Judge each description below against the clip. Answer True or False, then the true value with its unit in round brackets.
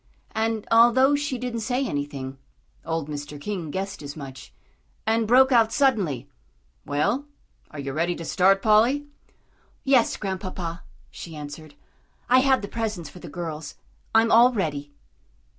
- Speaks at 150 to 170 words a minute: False (140 wpm)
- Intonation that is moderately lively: False (7.6 semitones)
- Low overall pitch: False (195 Hz)